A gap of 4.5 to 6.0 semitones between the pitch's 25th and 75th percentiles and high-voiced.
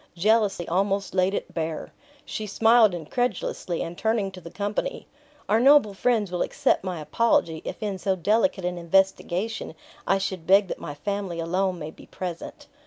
No: average, 3.5 semitones; high, 195 Hz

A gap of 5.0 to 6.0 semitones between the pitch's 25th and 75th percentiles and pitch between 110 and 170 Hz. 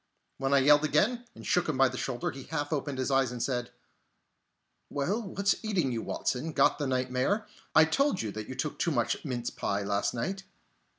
No: average, 4.5 semitones; low, 135 Hz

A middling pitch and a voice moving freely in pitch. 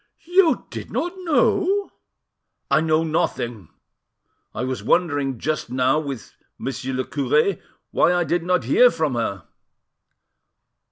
Yes: medium, 155 Hz; wide, 5.8 semitones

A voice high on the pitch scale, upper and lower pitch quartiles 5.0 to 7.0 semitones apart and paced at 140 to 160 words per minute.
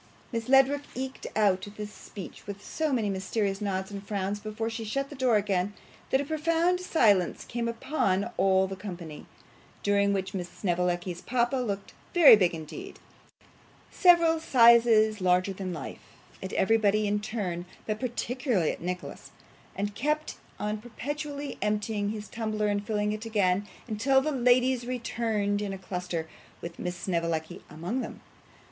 No: high, 210 Hz; average, 4.3 semitones; average, 155 wpm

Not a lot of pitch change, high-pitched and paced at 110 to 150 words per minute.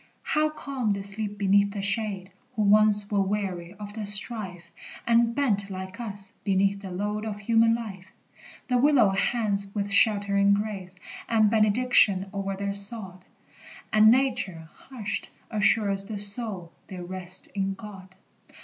Yes: narrow, 2.0 semitones; high, 200 Hz; average, 145 wpm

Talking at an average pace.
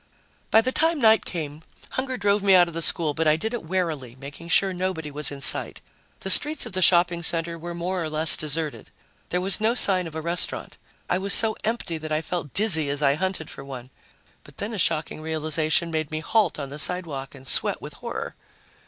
No: fast, 220 wpm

